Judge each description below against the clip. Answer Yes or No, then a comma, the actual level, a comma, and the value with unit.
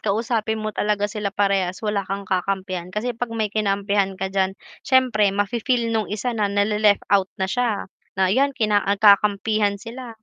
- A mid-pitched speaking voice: No, high, 205 Hz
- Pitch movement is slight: Yes, narrow, 2.1 semitones